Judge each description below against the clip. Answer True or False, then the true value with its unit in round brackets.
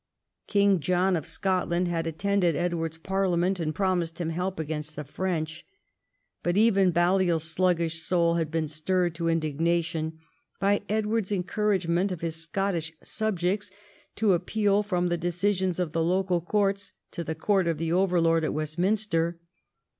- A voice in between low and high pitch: True (175 Hz)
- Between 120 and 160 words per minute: True (150 wpm)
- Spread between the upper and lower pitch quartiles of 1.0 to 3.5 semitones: True (2.7 semitones)